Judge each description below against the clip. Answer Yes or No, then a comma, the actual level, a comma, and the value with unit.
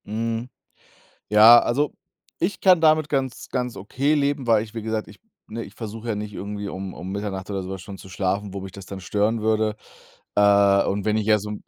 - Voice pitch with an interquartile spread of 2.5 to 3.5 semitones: Yes, average, 2.8 semitones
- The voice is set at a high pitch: No, low, 105 Hz